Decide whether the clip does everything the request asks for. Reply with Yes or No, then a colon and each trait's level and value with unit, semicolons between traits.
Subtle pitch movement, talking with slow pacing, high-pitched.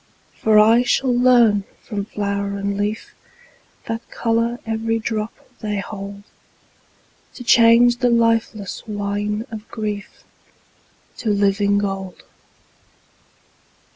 Yes: narrow, 2.2 semitones; slow, 105 wpm; high, 215 Hz